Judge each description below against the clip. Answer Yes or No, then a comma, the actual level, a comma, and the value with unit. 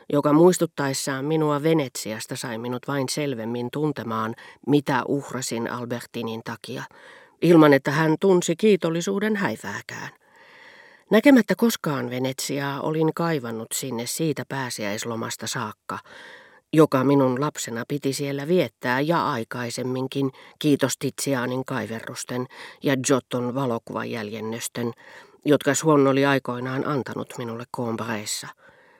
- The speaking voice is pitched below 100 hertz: No, low, 135 Hz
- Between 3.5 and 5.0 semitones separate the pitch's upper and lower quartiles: Yes, average, 3.9 semitones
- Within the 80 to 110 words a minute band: Yes, average, 100 wpm